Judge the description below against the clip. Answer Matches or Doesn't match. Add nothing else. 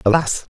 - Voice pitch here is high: Doesn't match